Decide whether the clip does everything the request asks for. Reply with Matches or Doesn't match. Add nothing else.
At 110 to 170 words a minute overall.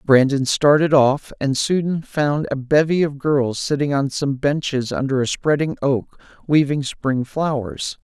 Matches